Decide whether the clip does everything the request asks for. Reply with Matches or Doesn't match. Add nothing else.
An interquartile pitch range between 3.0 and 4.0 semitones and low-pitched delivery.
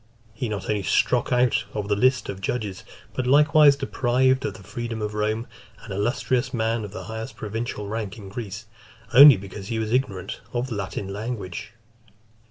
Matches